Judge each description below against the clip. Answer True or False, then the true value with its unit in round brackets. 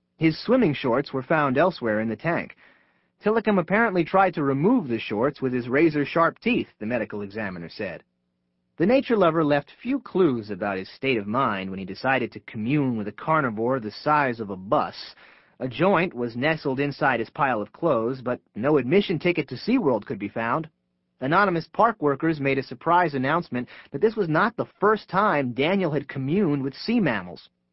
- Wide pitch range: True (7.0 semitones)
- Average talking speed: True (190 wpm)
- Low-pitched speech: False (145 Hz)